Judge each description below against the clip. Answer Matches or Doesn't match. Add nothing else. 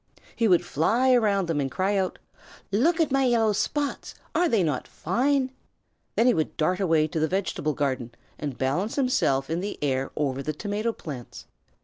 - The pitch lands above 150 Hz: Matches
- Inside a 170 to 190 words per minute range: Matches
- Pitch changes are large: Matches